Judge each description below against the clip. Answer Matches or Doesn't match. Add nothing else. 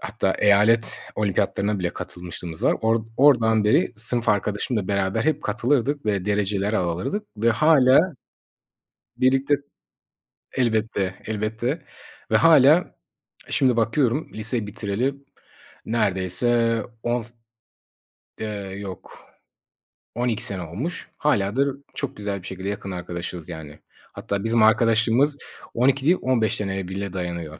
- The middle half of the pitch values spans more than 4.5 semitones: Doesn't match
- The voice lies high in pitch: Doesn't match